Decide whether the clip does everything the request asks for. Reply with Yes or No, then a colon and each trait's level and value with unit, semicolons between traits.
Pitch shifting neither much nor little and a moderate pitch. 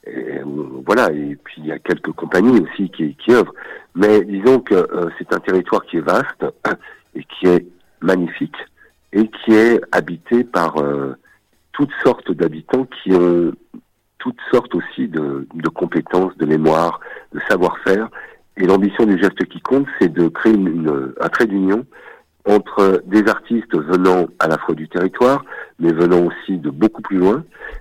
No: average, 4.0 semitones; very low, 95 Hz